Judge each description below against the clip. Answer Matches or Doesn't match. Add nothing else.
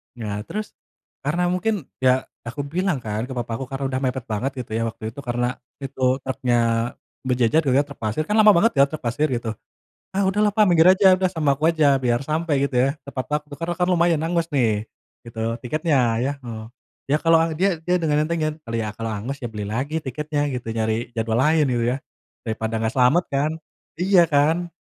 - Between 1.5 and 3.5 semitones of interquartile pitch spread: Doesn't match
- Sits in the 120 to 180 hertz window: Matches